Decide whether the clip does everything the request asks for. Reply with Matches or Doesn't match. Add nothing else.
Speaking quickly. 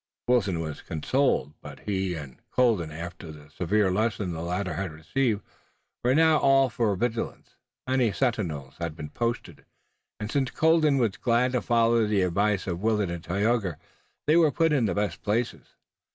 Doesn't match